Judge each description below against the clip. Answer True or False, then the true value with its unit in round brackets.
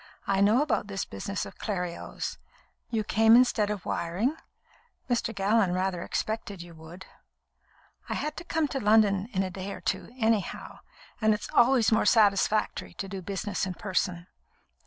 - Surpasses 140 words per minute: True (160 wpm)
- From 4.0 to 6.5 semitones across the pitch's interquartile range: False (2.9 semitones)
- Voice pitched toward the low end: False (205 Hz)